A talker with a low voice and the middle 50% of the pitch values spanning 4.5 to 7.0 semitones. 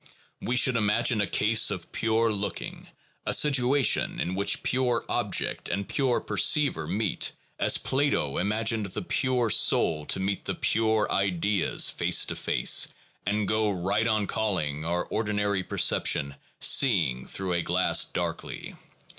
No: low, 105 Hz; average, 3.6 semitones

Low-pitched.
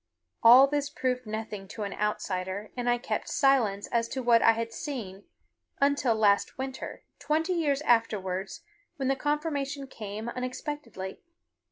No: high, 240 Hz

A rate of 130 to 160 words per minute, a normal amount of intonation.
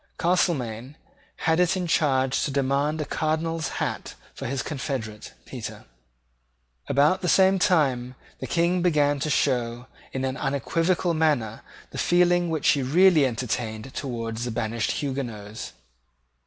Yes: slow, 135 wpm; average, 5.0 semitones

